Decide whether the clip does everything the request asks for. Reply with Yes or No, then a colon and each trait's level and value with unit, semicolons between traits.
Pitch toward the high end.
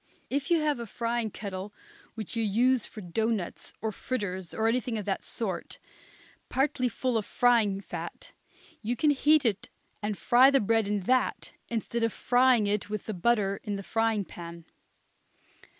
Yes: high, 225 Hz